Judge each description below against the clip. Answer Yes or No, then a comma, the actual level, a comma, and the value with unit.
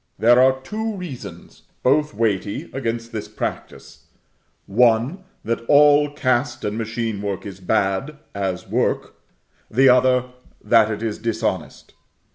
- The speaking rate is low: Yes, slow, 125 wpm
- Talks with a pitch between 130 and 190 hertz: No, low, 115 Hz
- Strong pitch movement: No, average, 3.7 semitones